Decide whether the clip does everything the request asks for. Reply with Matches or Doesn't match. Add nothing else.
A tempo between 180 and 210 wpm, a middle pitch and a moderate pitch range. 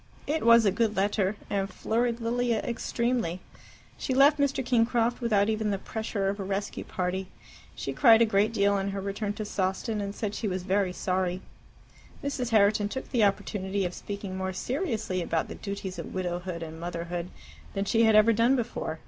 Doesn't match